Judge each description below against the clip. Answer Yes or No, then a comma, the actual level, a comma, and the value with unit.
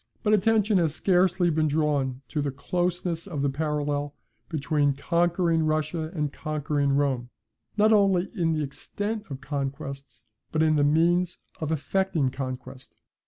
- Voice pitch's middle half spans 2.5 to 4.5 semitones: Yes, average, 3.8 semitones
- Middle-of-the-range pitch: Yes, medium, 155 Hz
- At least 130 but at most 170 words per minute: Yes, average, 145 wpm